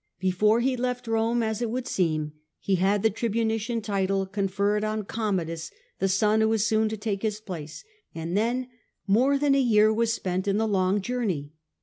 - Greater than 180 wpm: Yes, average, 190 wpm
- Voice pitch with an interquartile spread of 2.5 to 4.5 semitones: Yes, average, 2.9 semitones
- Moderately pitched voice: No, high, 215 Hz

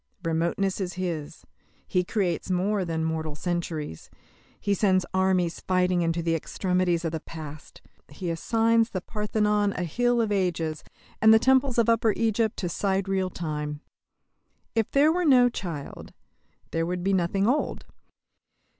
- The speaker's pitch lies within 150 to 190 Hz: Yes, medium, 185 Hz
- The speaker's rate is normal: Yes, average, 150 wpm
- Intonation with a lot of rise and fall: No, average, 4.2 semitones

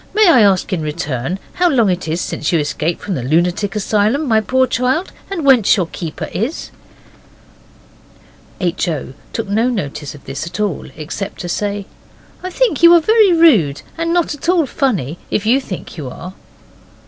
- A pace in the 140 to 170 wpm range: No, average, 185 wpm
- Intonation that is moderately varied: No, wide, 8.6 semitones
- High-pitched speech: Yes, high, 205 Hz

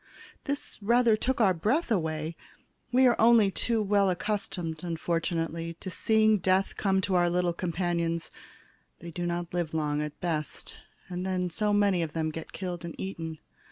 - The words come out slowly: No, average, 165 wpm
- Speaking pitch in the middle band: Yes, medium, 180 Hz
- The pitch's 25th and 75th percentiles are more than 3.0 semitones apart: Yes, average, 3.7 semitones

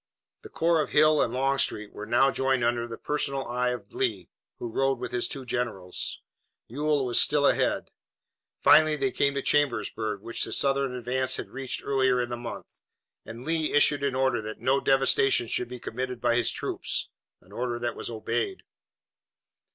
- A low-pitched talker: Yes, low, 125 Hz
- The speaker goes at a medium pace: Yes, average, 180 wpm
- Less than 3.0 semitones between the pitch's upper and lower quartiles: Yes, narrow, 2.6 semitones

